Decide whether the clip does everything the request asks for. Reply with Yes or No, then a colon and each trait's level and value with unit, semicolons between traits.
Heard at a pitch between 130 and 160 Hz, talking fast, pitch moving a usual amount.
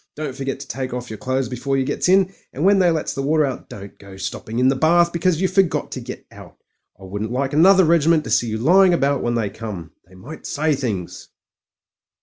No: low, 135 Hz; fast, 230 wpm; wide, 5.9 semitones